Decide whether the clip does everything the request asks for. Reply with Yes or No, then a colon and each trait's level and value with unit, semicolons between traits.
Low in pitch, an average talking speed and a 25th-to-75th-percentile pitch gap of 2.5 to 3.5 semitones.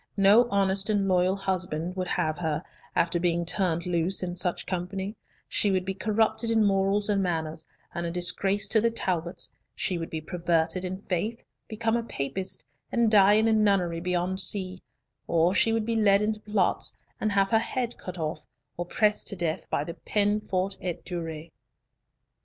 No: high, 190 Hz; average, 180 wpm; average, 3.1 semitones